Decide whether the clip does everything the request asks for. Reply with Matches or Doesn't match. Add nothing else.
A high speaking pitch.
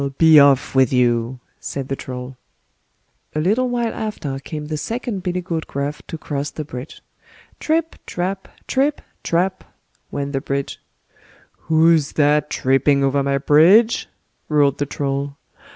Doesn't match